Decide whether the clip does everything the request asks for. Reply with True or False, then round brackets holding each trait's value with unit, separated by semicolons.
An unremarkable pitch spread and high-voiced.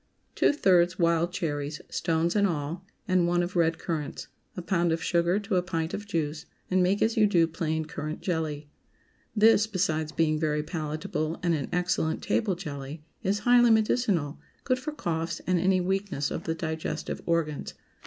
False (3.1 semitones; 170 Hz)